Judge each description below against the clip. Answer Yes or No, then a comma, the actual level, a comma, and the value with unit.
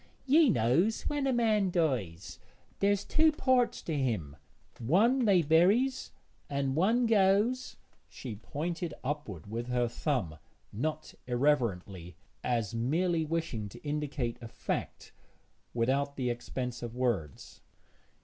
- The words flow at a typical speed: No, slow, 130 wpm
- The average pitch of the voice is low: No, medium, 145 Hz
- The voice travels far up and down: Yes, wide, 8.6 semitones